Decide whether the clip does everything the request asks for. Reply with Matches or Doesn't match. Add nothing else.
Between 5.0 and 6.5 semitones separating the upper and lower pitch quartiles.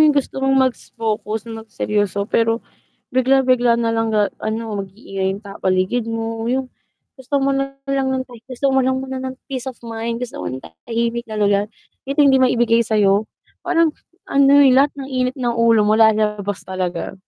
Doesn't match